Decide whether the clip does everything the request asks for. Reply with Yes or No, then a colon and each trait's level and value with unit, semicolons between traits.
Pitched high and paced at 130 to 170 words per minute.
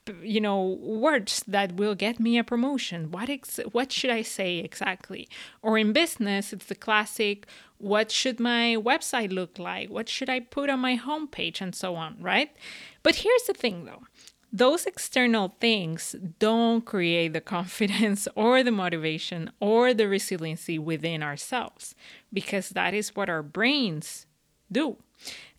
Yes: high, 215 Hz; average, 155 wpm